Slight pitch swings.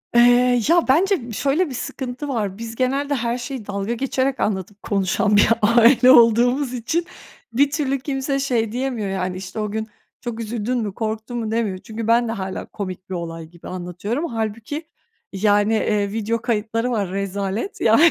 No: average, 3.8 semitones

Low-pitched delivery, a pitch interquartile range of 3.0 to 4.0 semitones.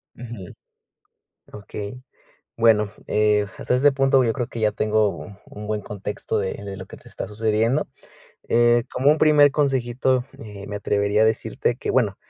Yes: low, 110 Hz; average, 3.4 semitones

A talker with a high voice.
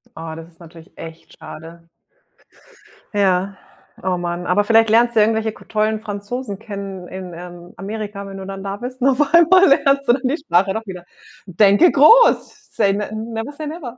Yes: high, 205 Hz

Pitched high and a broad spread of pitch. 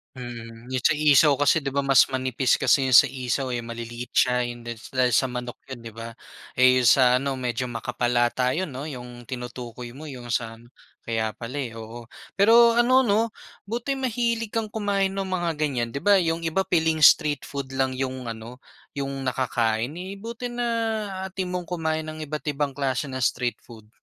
No: low, 135 Hz; wide, 6.5 semitones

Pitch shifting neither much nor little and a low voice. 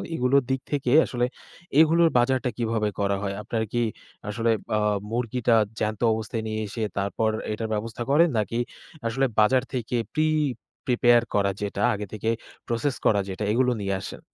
Yes: average, 3.1 semitones; low, 115 Hz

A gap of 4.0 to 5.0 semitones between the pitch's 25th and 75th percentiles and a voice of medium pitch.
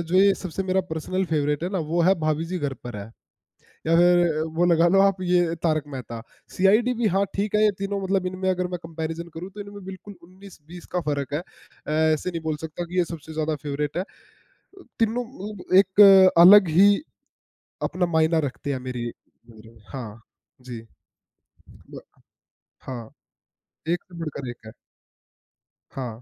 Yes: average, 4.3 semitones; medium, 170 Hz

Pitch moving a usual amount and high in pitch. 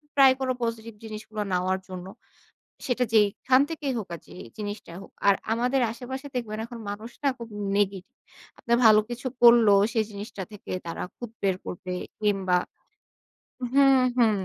Yes: average, 3.6 semitones; high, 220 Hz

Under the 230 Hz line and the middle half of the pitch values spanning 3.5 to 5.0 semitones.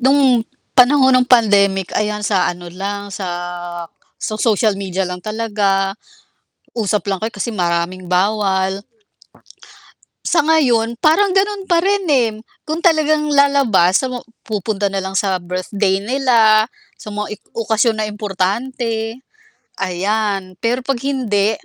Yes: high, 215 Hz; average, 4.6 semitones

